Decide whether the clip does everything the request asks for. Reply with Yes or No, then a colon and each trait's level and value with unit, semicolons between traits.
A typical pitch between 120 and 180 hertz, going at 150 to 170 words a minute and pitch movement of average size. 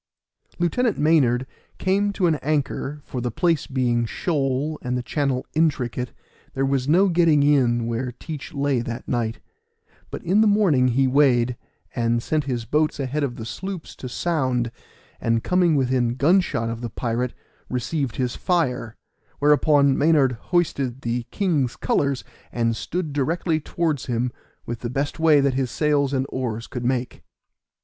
Yes: low, 135 Hz; average, 160 wpm; average, 4.2 semitones